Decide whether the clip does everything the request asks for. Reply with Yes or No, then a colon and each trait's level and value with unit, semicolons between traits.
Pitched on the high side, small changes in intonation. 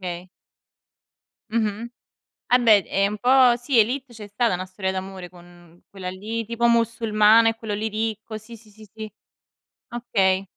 No: high, 215 Hz; average, 3.2 semitones